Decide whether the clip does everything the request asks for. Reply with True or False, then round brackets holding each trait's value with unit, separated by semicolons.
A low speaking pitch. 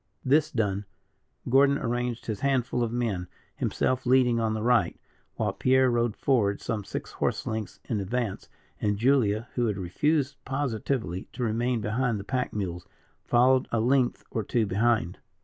True (120 Hz)